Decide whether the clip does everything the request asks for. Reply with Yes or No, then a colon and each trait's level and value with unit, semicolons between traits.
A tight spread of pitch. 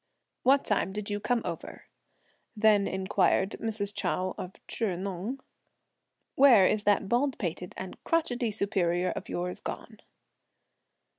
No: average, 3.4 semitones